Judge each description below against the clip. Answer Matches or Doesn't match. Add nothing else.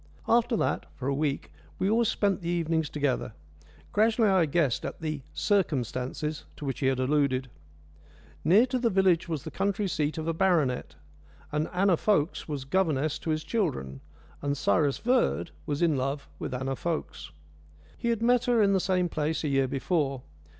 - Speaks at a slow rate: Doesn't match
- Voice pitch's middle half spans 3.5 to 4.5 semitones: Doesn't match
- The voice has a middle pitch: Matches